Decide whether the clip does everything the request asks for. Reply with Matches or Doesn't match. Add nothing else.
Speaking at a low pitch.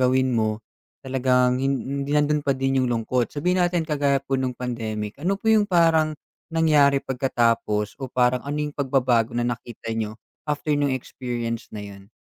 Matches